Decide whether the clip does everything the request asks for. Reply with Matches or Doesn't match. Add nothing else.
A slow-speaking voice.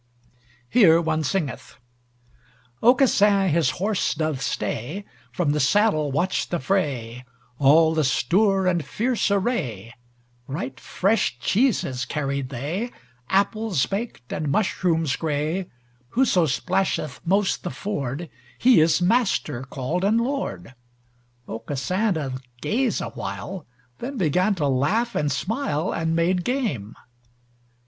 Matches